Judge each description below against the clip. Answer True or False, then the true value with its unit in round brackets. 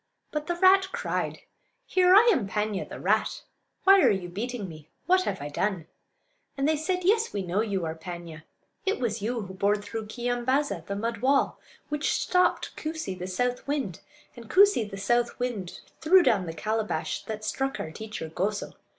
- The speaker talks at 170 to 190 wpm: True (185 wpm)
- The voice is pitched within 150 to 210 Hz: False (225 Hz)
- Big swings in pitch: True (7.5 semitones)